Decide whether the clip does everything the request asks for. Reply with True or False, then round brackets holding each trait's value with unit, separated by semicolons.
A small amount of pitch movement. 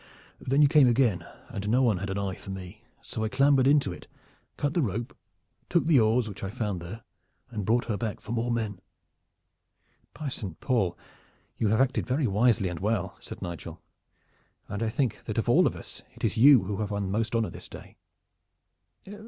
False (4.1 semitones)